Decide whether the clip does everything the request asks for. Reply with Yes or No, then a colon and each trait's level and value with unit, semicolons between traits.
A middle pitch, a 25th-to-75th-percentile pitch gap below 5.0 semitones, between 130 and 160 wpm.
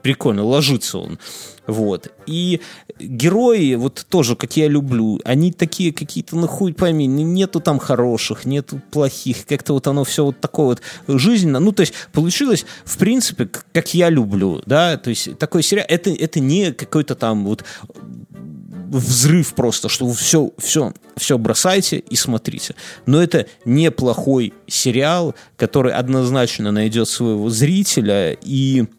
No: medium, 145 Hz; wide, 5.5 semitones; average, 145 wpm